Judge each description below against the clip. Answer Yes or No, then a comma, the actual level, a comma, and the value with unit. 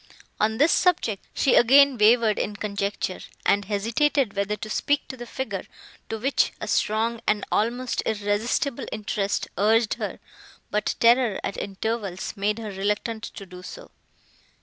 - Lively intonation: No, average, 2.8 semitones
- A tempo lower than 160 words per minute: Yes, average, 150 wpm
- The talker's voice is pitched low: No, high, 215 Hz